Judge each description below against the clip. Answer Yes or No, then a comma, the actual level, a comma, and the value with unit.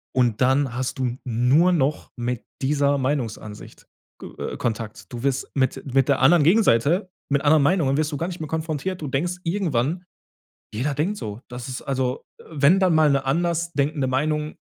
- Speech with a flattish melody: No, average, 3.9 semitones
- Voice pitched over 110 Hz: Yes, medium, 140 Hz